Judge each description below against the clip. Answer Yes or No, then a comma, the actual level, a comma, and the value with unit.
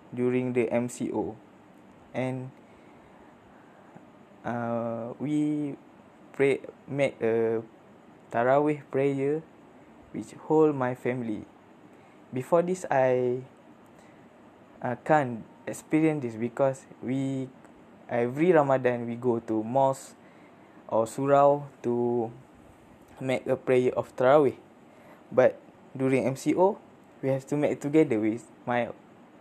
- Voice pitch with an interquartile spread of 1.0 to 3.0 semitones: Yes, average, 2.7 semitones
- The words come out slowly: Yes, slow, 95 wpm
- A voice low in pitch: Yes, low, 130 Hz